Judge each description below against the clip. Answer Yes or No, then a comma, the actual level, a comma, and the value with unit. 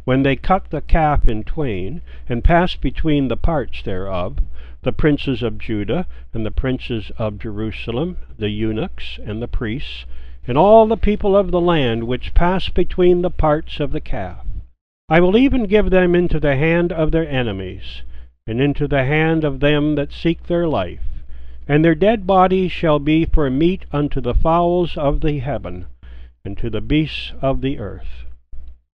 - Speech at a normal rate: Yes, average, 175 wpm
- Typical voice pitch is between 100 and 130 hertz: No, medium, 140 Hz